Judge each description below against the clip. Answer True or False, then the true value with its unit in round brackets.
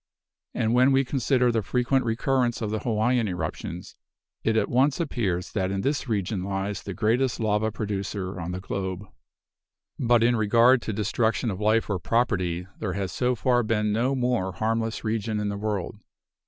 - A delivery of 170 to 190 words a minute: True (175 wpm)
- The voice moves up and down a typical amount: True (3.6 semitones)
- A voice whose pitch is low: True (110 Hz)